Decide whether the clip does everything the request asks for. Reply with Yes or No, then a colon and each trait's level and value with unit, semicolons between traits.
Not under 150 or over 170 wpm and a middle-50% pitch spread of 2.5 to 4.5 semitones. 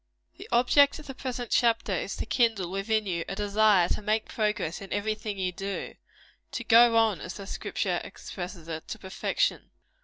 No: average, 185 wpm; average, 3.2 semitones